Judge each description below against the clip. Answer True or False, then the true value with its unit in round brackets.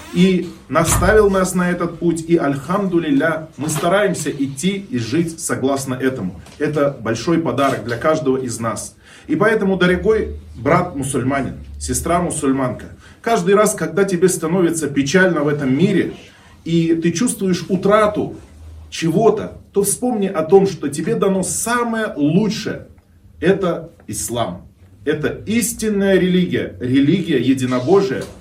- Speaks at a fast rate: False (120 wpm)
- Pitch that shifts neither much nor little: False (6.6 semitones)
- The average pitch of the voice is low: False (165 Hz)